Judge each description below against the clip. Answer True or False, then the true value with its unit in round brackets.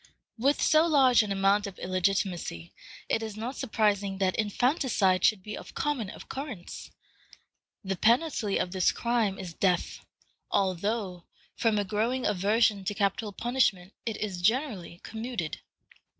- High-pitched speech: True (205 Hz)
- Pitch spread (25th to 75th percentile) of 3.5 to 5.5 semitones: True (3.8 semitones)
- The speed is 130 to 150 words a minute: True (135 wpm)